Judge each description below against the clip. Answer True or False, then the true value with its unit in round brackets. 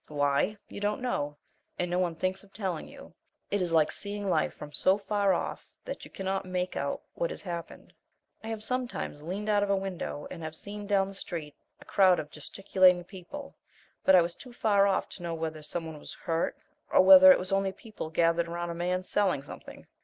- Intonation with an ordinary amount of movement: True (3.3 semitones)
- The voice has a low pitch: False (185 Hz)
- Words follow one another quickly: True (215 wpm)